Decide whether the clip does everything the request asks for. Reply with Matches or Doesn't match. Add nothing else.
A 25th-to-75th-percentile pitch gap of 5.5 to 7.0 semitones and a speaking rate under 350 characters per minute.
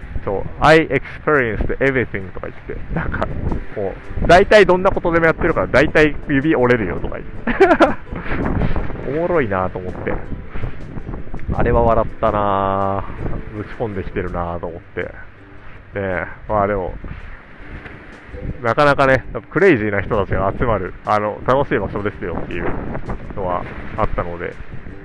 Matches